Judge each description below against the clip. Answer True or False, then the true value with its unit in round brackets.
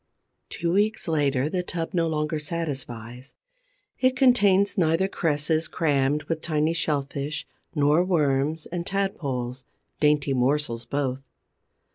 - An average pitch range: True (3.5 semitones)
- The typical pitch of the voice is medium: True (150 Hz)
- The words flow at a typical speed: False (115 wpm)